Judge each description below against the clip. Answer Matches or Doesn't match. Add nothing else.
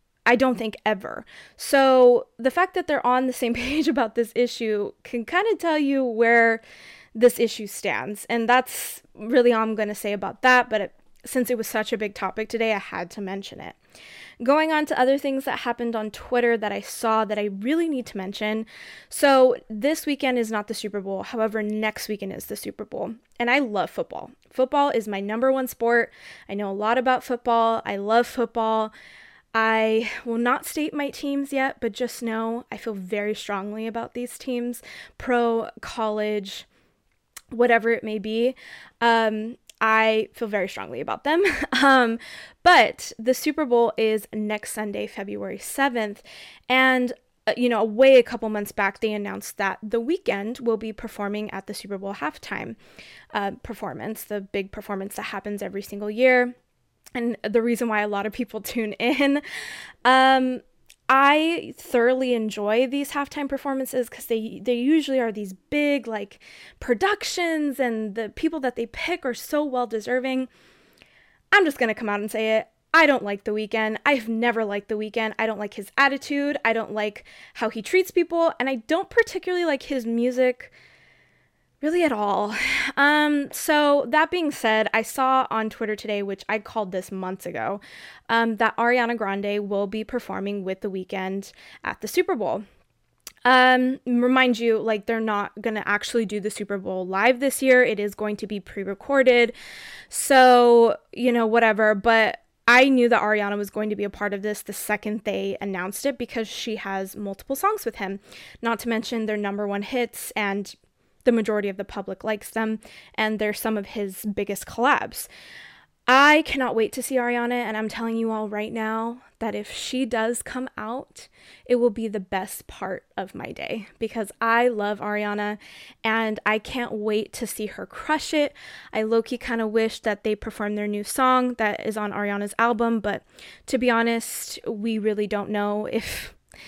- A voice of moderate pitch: Doesn't match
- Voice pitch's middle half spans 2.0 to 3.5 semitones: Matches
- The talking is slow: Doesn't match